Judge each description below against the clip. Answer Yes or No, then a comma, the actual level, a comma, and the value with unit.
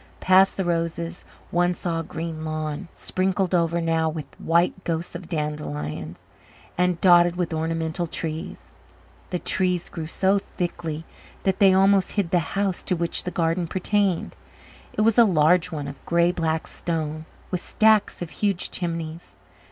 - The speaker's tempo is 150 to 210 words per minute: Yes, average, 160 wpm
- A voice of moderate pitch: Yes, medium, 170 Hz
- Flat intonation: Yes, narrow, 2.3 semitones